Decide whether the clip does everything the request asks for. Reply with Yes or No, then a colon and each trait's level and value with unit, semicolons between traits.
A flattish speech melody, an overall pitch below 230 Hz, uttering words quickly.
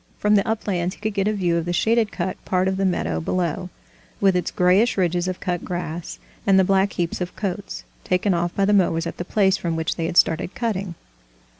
Yes: narrow, 2.2 semitones; medium, 185 Hz; fast, 230 wpm